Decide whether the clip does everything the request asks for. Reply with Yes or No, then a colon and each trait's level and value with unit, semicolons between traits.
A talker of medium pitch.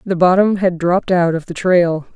Yes: medium, 180 Hz